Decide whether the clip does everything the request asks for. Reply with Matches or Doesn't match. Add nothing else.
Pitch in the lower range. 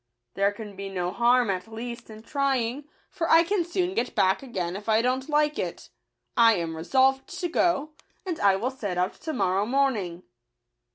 Doesn't match